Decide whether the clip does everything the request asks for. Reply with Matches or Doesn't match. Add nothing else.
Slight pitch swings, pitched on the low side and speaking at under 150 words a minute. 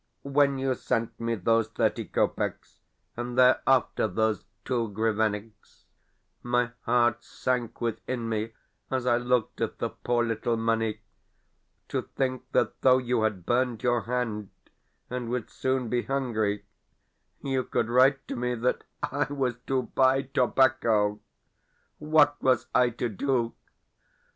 Matches